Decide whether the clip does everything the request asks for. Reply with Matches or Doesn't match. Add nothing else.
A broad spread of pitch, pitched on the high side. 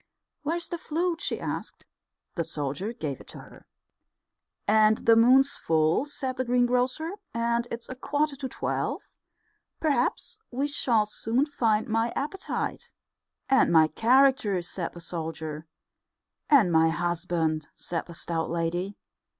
Matches